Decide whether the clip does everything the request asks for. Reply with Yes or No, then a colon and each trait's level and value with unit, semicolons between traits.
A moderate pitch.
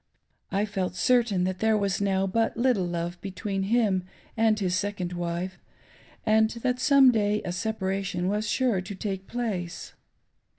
No: high, 200 Hz